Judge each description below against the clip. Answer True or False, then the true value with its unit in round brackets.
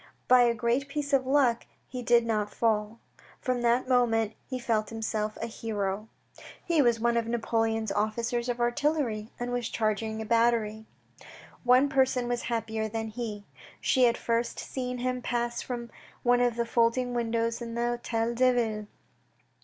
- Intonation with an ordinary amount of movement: False (1.7 semitones)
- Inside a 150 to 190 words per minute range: True (160 wpm)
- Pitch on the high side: True (235 Hz)